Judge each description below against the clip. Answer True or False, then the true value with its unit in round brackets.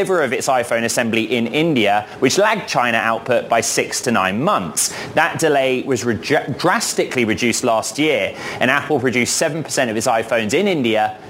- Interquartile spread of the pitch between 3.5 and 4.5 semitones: False (4.9 semitones)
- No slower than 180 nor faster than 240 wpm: False (170 wpm)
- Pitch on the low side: True (120 Hz)